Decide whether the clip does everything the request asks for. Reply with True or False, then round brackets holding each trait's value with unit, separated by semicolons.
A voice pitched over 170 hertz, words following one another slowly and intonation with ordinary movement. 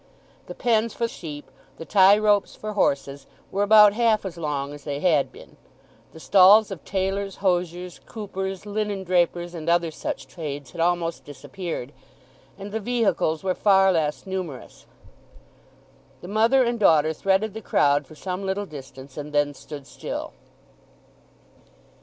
False (185 Hz; 150 wpm; 4.8 semitones)